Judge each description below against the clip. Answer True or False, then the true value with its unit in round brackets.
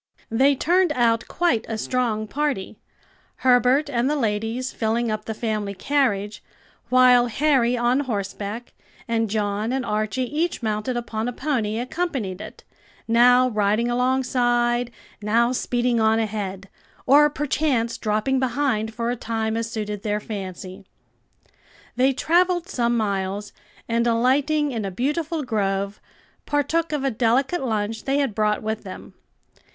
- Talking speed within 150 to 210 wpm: False (140 wpm)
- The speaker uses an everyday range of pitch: True (3.6 semitones)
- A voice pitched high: True (235 Hz)